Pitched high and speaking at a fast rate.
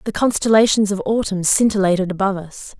No: high, 200 Hz; average, 150 wpm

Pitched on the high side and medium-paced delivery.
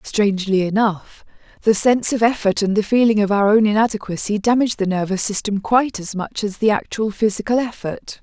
Yes: high, 210 Hz; average, 180 wpm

